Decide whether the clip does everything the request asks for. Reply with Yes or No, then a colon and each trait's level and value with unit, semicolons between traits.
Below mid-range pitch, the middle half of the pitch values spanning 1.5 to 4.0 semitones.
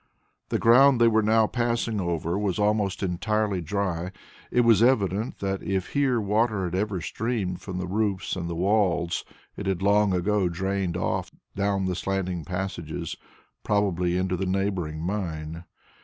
Yes: very low, 95 Hz; average, 2.9 semitones